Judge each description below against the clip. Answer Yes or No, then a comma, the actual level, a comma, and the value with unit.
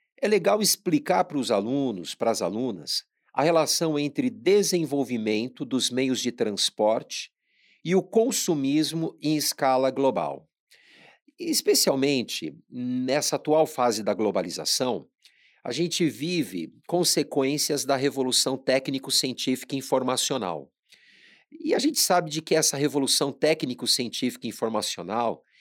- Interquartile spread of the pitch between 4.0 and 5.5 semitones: Yes, average, 4.7 semitones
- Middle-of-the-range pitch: Yes, medium, 145 Hz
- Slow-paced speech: Yes, slow, 115 wpm